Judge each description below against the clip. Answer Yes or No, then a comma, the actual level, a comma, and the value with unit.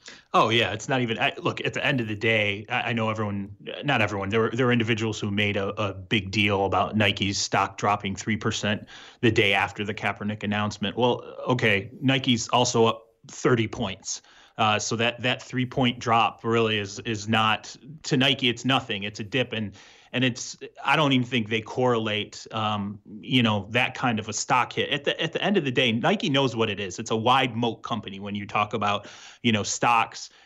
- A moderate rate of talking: No, fast, 215 wpm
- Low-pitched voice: Yes, low, 115 Hz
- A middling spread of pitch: Yes, average, 3.0 semitones